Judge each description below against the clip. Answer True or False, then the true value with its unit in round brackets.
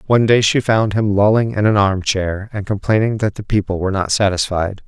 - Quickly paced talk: True (220 wpm)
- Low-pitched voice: True (105 Hz)